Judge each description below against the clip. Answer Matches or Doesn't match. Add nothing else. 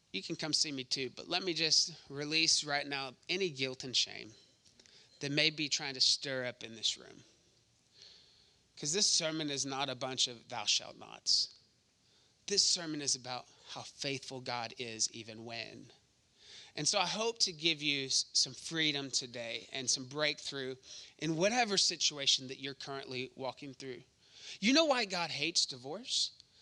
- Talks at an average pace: Matches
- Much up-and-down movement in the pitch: Doesn't match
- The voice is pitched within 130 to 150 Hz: Matches